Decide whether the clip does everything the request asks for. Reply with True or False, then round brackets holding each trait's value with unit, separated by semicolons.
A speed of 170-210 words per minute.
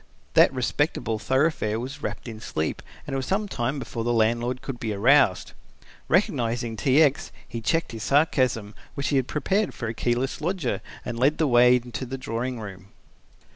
True (180 wpm)